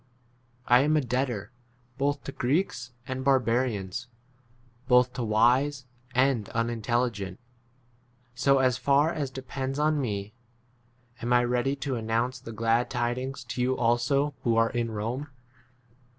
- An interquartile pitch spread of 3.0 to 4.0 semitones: No, narrow, 2.6 semitones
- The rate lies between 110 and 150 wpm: Yes, slow, 135 wpm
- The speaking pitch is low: Yes, low, 125 Hz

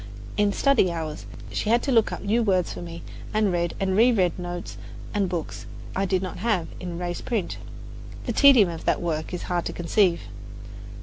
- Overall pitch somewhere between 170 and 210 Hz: Yes, medium, 185 Hz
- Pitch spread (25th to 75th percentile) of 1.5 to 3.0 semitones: No, average, 3.6 semitones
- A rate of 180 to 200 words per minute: Yes, average, 190 wpm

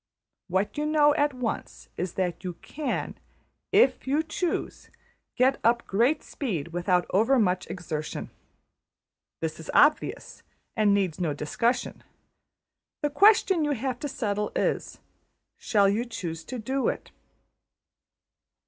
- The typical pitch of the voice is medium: No, high, 230 Hz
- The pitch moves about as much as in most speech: No, wide, 7.4 semitones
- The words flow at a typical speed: No, slow, 125 wpm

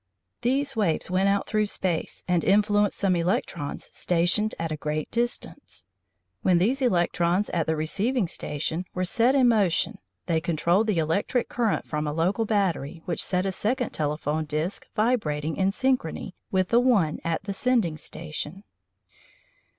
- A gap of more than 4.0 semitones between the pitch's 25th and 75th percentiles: Yes, average, 4.9 semitones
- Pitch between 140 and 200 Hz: Yes, medium, 185 Hz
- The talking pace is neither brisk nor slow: Yes, average, 155 wpm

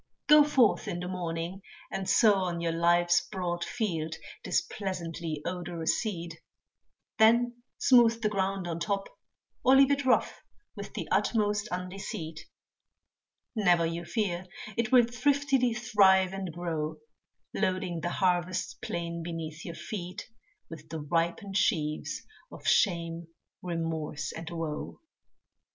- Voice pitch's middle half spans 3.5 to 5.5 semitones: Yes, average, 3.9 semitones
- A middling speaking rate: No, slow, 130 wpm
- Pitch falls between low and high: Yes, medium, 180 Hz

